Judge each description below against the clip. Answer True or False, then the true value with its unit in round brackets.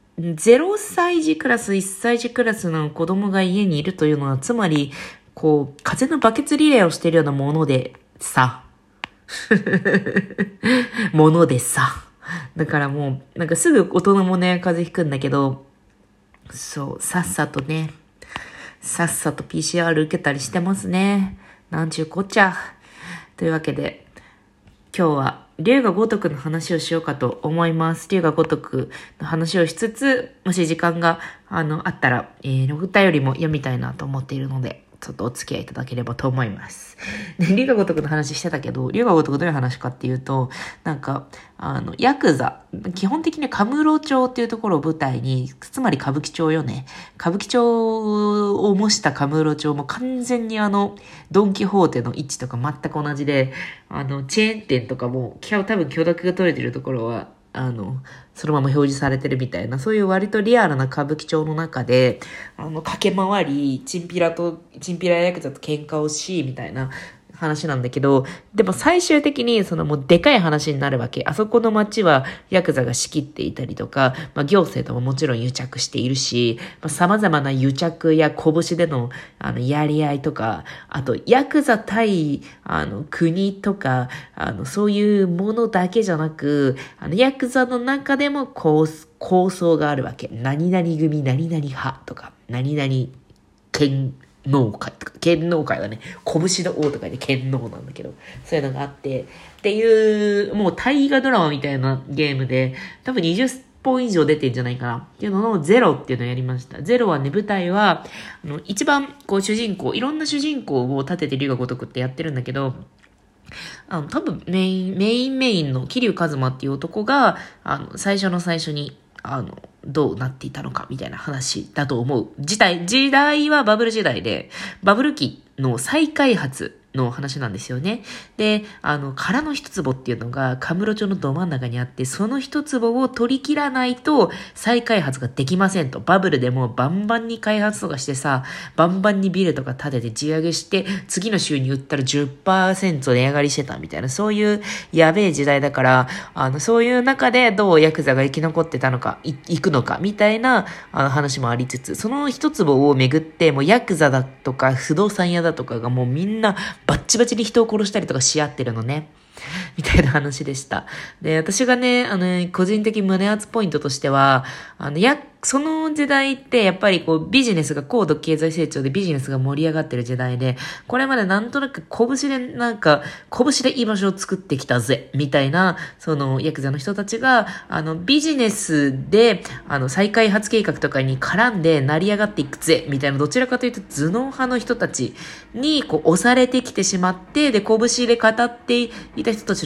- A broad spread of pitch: True (7.2 semitones)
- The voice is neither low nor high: True (165 Hz)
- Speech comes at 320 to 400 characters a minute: True (345 characters per minute)